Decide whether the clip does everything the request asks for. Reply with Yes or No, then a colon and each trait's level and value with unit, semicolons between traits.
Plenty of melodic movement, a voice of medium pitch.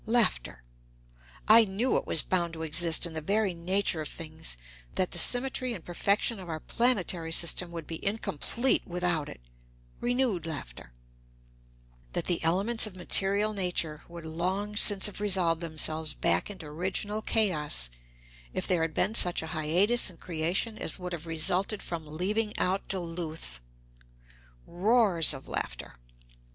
No: average, 4.2 semitones; medium, 180 Hz